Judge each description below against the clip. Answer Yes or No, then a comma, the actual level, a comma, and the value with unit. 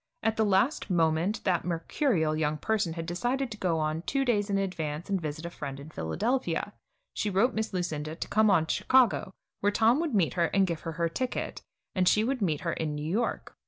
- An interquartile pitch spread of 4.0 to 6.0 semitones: Yes, wide, 5.4 semitones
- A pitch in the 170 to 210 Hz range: Yes, medium, 185 Hz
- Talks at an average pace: No, fast, 225 wpm